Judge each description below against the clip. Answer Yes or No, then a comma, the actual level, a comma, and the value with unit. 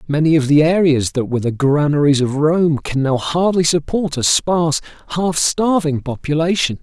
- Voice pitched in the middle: Yes, medium, 155 Hz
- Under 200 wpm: Yes, average, 165 wpm